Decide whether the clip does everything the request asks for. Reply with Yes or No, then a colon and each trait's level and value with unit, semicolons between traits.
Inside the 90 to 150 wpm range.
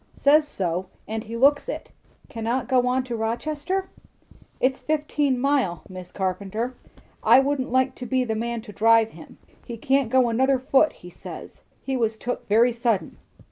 No: average, 170 wpm